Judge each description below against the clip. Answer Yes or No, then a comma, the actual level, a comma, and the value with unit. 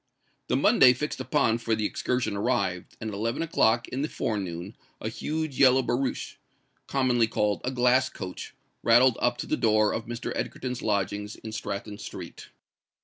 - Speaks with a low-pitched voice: Yes, low, 115 Hz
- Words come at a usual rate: Yes, average, 165 wpm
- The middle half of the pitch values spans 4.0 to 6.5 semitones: No, average, 3.3 semitones